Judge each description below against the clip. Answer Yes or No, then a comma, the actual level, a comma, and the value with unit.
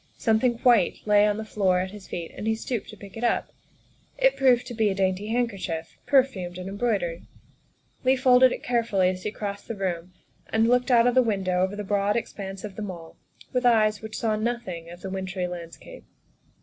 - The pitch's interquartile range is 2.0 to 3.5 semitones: No, average, 4.0 semitones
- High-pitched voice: Yes, high, 210 Hz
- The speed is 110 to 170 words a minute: No, fast, 205 wpm